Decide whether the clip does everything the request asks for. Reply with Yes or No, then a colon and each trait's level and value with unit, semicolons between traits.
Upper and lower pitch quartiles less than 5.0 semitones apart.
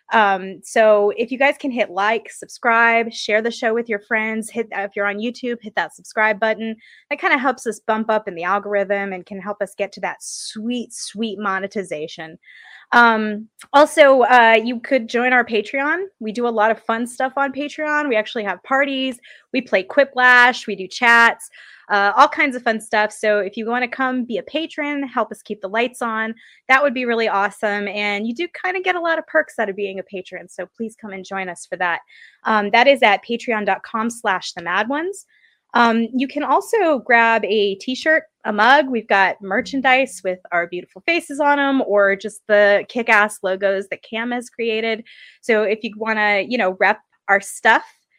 Yes: average, 4.1 semitones